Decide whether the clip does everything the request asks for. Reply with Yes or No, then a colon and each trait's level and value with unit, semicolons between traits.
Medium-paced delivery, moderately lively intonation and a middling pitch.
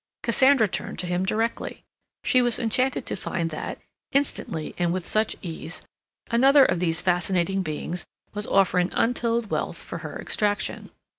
No: average, 150 wpm; average, 4.8 semitones; high, 195 Hz